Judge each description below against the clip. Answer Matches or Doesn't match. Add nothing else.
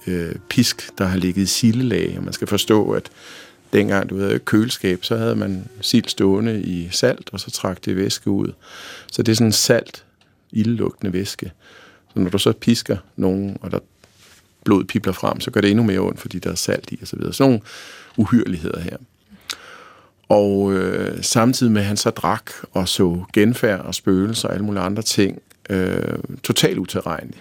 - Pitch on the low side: Matches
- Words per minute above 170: Matches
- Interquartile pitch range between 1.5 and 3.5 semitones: Matches